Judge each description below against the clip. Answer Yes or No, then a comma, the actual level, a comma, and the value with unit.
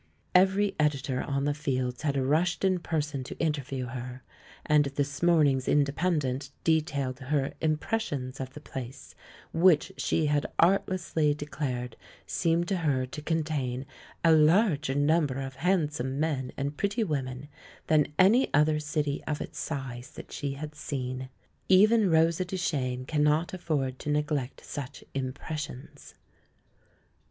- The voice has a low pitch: No, medium, 150 Hz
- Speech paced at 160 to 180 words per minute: No, slow, 135 wpm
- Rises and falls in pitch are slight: No, average, 3.4 semitones